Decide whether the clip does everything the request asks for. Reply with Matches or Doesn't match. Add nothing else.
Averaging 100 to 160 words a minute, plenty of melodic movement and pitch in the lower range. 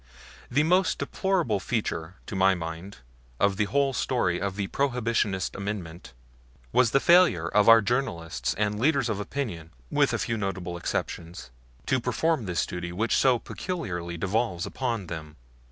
Matches